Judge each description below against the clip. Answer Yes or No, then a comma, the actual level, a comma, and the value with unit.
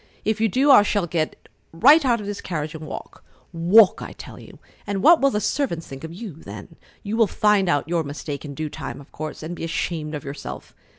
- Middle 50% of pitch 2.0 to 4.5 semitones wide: No, wide, 5.5 semitones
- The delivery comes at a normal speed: No, fast, 230 wpm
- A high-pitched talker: No, medium, 170 Hz